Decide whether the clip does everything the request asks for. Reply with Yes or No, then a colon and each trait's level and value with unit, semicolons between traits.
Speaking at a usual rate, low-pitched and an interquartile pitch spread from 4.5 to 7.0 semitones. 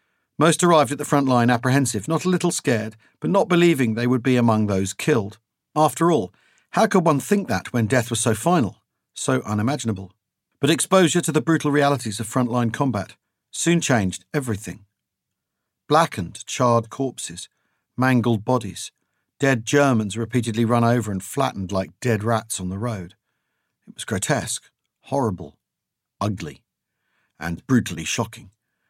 Yes: average, 150 wpm; low, 120 Hz; average, 4.9 semitones